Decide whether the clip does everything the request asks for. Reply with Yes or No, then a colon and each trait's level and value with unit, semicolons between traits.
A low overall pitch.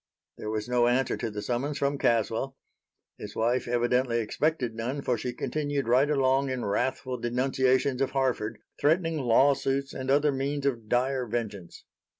Yes: low, 130 Hz